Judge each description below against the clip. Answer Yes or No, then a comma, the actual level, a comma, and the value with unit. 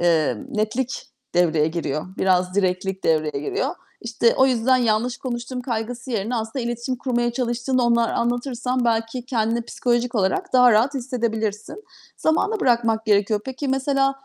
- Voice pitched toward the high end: Yes, high, 235 Hz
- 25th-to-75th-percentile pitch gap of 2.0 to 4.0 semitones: Yes, average, 2.9 semitones